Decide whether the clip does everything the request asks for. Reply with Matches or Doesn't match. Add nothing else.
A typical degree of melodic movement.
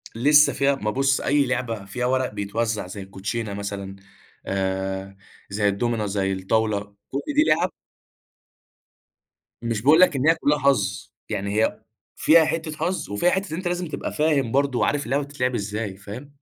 Doesn't match